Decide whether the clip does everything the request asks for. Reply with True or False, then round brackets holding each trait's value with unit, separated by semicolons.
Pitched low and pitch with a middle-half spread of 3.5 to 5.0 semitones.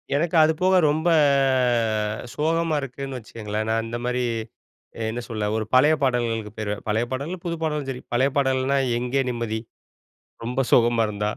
True (125 Hz; 3.9 semitones)